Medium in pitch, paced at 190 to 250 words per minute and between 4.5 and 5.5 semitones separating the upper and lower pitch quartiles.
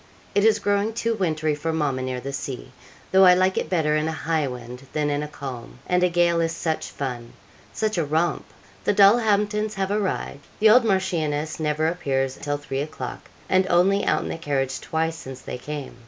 Yes: medium, 160 Hz; average, 200 wpm; average, 4.9 semitones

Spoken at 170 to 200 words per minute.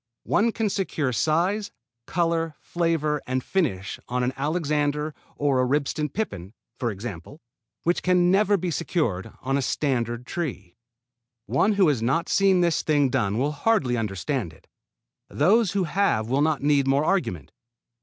No: average, 155 wpm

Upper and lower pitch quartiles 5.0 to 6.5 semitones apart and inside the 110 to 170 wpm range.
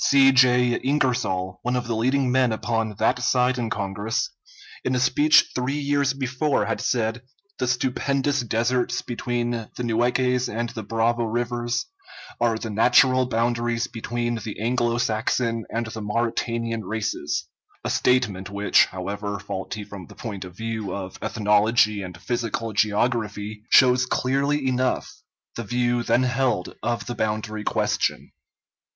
No: narrow, 2.6 semitones; average, 145 wpm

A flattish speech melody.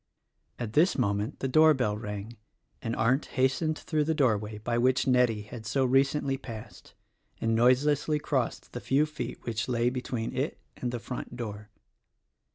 No: average, 3.3 semitones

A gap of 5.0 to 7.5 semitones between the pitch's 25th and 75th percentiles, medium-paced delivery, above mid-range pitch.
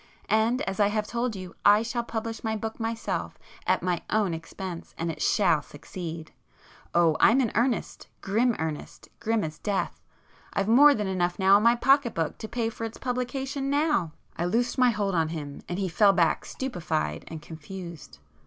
Yes: wide, 5.4 semitones; average, 175 wpm; high, 205 Hz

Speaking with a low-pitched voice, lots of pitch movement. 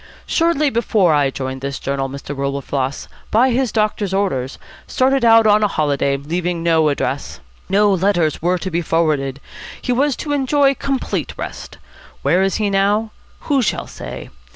No: high, 190 Hz; wide, 8.0 semitones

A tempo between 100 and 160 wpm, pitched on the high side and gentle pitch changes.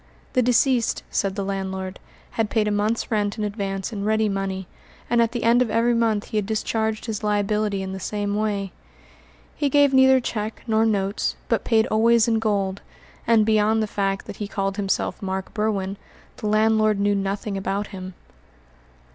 No: average, 180 wpm; high, 210 Hz; narrow, 2.1 semitones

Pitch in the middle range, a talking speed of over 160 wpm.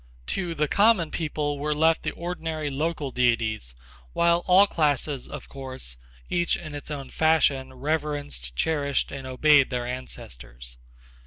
No: medium, 145 Hz; average, 140 wpm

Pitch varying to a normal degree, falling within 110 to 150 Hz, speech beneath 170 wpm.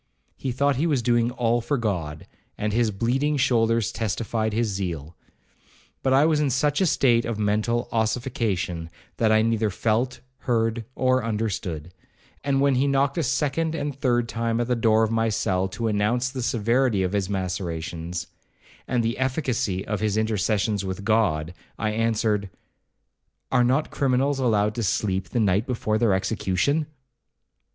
Yes: average, 3.7 semitones; low, 115 Hz; average, 160 wpm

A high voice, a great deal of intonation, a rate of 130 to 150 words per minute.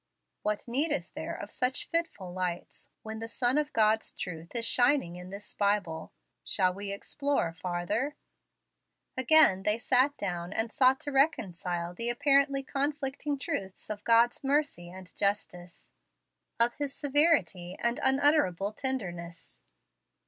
Yes: high, 225 Hz; wide, 7.1 semitones; slow, 135 wpm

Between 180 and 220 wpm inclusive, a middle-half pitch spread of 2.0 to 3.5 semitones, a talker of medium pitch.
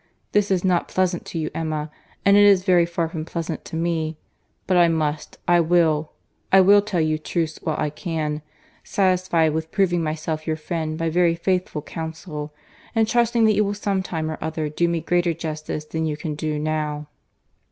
Yes: average, 185 wpm; average, 2.7 semitones; medium, 165 Hz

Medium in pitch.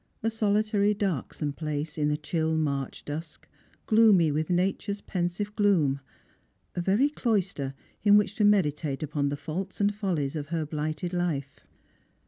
Yes: medium, 170 Hz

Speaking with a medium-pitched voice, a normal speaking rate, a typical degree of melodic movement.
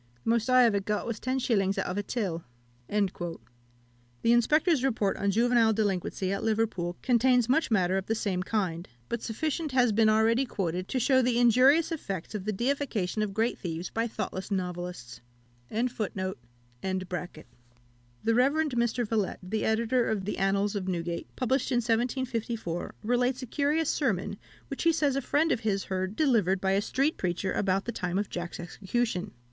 No: high, 215 Hz; average, 170 wpm; average, 4.8 semitones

